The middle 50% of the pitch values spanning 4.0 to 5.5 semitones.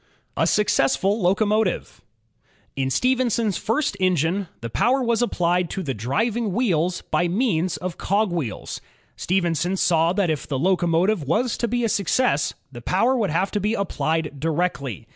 Yes: average, 5.0 semitones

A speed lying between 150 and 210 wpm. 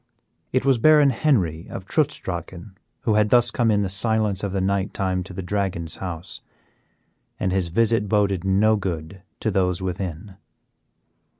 Yes: average, 165 wpm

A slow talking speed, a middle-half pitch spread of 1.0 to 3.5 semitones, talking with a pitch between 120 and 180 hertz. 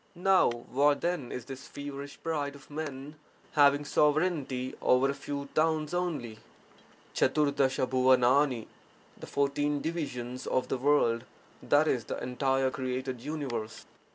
Yes: slow, 130 wpm; narrow, 2.4 semitones; medium, 140 Hz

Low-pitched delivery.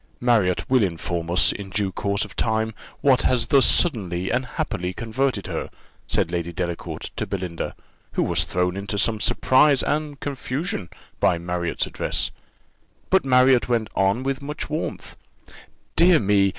Yes: low, 110 Hz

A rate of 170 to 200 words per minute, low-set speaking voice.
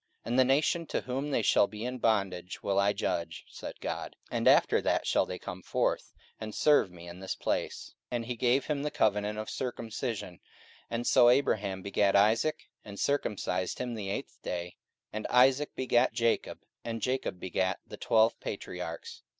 Yes: average, 185 wpm; low, 110 Hz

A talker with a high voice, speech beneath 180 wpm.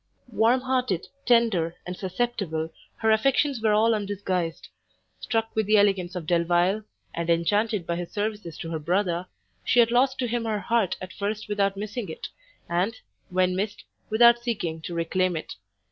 Yes: high, 205 Hz; average, 165 wpm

